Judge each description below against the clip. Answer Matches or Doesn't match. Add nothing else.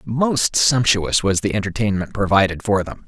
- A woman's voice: Doesn't match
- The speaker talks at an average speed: Matches